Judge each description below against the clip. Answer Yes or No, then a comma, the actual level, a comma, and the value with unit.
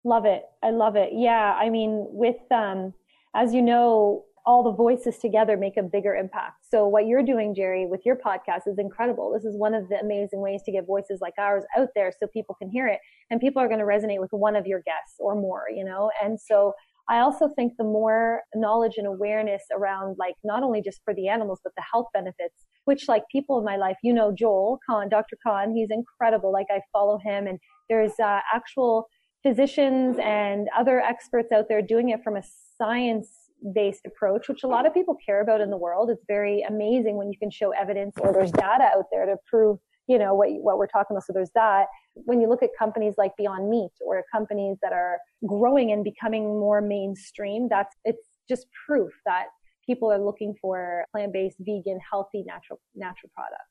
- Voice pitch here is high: Yes, high, 210 Hz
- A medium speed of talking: No, fast, 210 wpm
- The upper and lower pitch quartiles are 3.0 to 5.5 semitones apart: No, narrow, 2.5 semitones